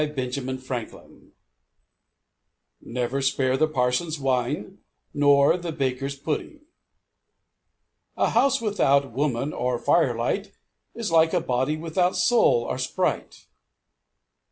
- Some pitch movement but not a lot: Yes, average, 4.6 semitones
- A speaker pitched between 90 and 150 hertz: Yes, medium, 140 Hz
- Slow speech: Yes, slow, 105 wpm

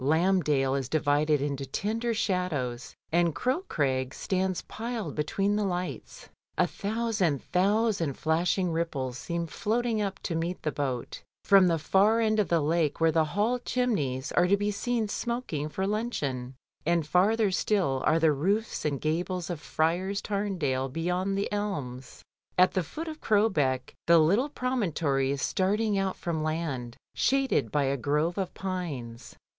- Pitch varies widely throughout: Yes, wide, 5.7 semitones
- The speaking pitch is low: No, medium, 175 Hz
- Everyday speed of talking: Yes, average, 155 wpm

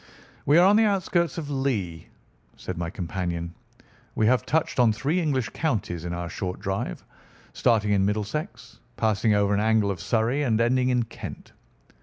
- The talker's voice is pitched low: Yes, low, 110 Hz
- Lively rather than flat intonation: Yes, wide, 5.9 semitones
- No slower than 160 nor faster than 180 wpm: Yes, average, 170 wpm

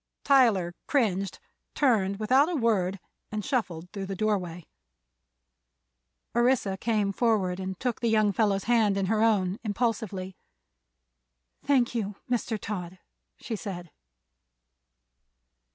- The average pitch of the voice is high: Yes, high, 210 Hz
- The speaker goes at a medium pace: No, slow, 115 wpm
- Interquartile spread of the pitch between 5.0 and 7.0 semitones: No, average, 3.5 semitones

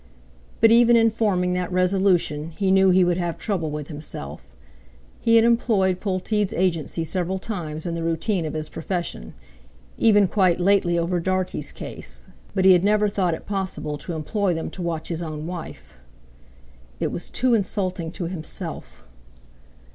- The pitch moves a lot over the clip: No, average, 3.2 semitones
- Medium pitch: Yes, medium, 180 Hz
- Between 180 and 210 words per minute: No, average, 160 wpm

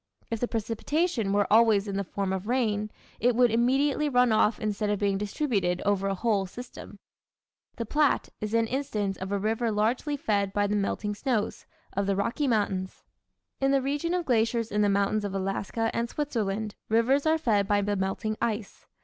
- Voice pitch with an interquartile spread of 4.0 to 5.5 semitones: No, average, 3.4 semitones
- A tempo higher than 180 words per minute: Yes, average, 190 wpm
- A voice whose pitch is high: Yes, high, 215 Hz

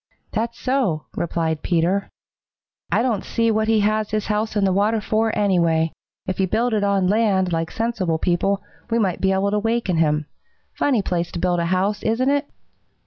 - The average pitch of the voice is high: Yes, high, 200 Hz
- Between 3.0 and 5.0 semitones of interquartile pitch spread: Yes, average, 4.0 semitones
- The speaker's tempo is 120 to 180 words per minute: No, average, 195 wpm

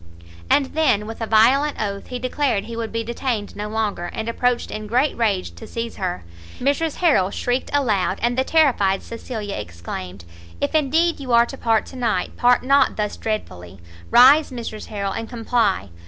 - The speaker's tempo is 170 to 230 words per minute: Yes, average, 180 wpm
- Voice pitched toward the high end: Yes, high, 230 Hz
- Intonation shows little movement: No, average, 4.0 semitones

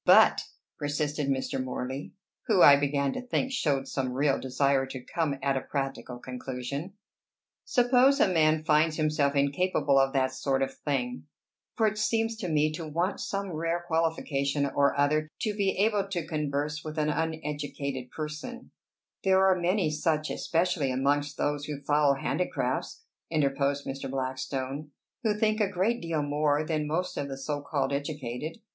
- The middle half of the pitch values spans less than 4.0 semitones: Yes, average, 3.3 semitones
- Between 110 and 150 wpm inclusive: No, average, 160 wpm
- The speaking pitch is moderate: Yes, medium, 150 Hz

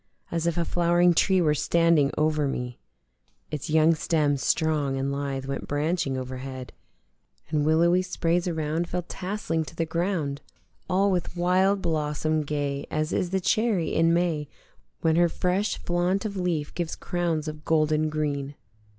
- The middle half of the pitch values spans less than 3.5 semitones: Yes, average, 2.8 semitones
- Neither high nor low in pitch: Yes, medium, 160 Hz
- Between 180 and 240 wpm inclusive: No, average, 155 wpm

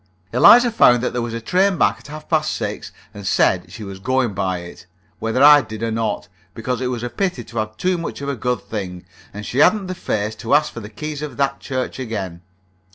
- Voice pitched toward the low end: Yes, low, 120 Hz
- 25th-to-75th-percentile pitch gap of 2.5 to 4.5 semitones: No, wide, 5.4 semitones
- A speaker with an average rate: No, fast, 235 wpm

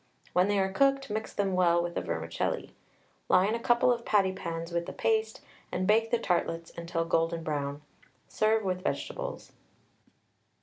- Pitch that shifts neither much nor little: Yes, average, 4.5 semitones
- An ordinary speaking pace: Yes, average, 165 wpm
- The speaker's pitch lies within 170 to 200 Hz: Yes, high, 190 Hz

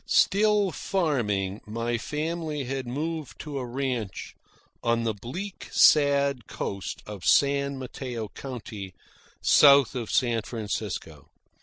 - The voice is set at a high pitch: No, low, 130 Hz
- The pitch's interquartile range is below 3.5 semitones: No, average, 4.4 semitones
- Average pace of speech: No, slow, 115 wpm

